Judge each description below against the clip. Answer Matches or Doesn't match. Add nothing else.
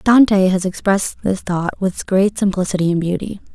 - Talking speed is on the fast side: Doesn't match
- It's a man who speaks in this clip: Doesn't match